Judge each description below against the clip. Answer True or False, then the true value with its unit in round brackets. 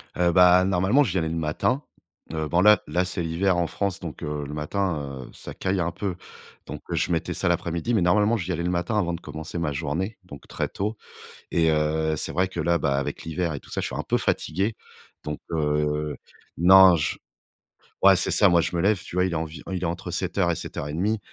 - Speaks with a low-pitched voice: True (85 Hz)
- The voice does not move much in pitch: False (3.2 semitones)